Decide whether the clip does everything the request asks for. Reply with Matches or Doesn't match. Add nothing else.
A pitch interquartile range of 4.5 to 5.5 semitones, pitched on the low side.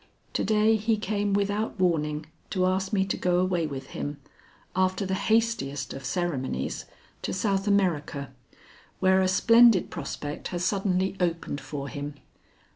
Doesn't match